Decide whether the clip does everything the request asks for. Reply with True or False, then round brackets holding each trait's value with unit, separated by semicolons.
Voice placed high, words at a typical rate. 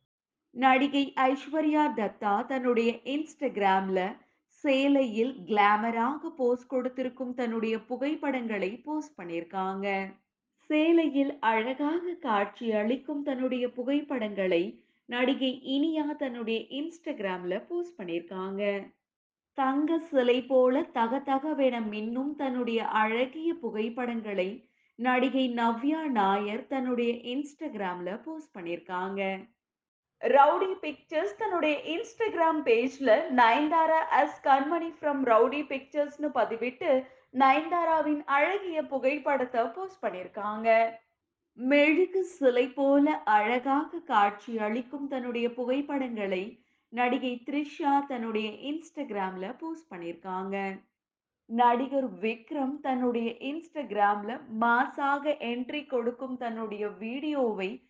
True (255 Hz; 85 wpm)